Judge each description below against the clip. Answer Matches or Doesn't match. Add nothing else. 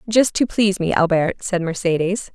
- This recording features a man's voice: Doesn't match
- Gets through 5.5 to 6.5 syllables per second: Doesn't match